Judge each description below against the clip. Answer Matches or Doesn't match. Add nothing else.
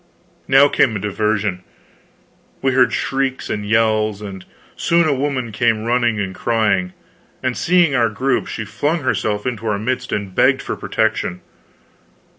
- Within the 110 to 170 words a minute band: Matches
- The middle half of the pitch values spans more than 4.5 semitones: Doesn't match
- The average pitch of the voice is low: Matches